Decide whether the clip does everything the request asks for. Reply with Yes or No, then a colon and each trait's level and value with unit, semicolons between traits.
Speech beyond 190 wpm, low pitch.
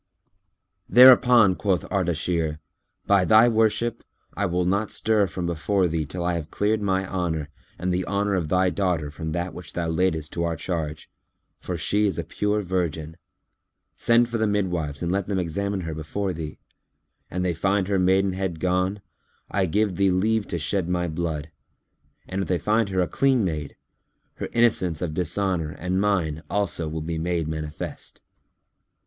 No: average, 170 wpm; very low, 90 Hz